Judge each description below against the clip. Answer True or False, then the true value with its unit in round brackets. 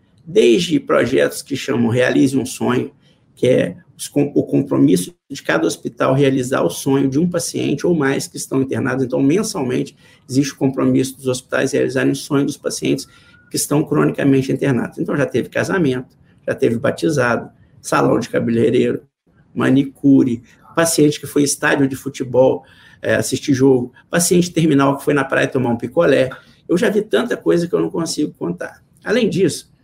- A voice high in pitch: False (135 Hz)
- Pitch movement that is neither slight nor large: False (1.7 semitones)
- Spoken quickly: False (165 wpm)